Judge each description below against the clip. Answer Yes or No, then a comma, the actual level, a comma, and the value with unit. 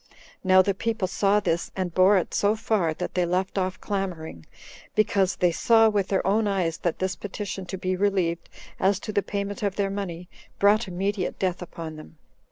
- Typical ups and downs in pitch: No, narrow, 2.2 semitones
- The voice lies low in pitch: No, high, 190 Hz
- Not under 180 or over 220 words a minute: Yes, average, 190 wpm